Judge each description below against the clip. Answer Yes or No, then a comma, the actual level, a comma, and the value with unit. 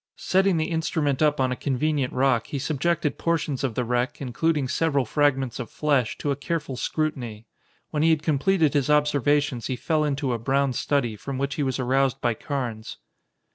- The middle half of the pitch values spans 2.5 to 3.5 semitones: Yes, average, 3.0 semitones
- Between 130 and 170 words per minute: No, average, 185 wpm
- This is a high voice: No, medium, 140 Hz